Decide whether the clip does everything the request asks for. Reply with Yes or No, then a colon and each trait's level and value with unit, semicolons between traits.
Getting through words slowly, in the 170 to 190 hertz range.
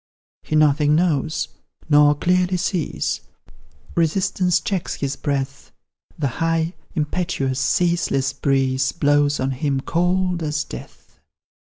No: slow, 110 wpm; medium, 150 Hz